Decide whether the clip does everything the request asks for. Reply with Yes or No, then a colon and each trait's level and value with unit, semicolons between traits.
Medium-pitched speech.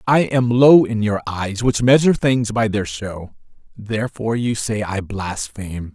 No: low, 110 Hz